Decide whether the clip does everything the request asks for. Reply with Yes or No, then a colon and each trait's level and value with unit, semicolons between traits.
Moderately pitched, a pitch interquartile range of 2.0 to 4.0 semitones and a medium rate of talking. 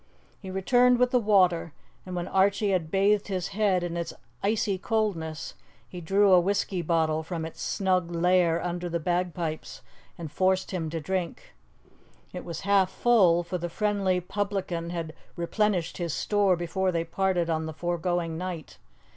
Yes: medium, 180 Hz; narrow, 2.5 semitones; average, 165 wpm